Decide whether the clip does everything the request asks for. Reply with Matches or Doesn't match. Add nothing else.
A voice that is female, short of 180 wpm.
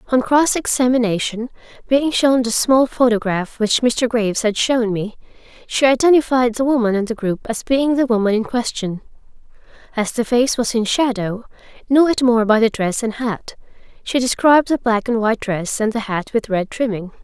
Doesn't match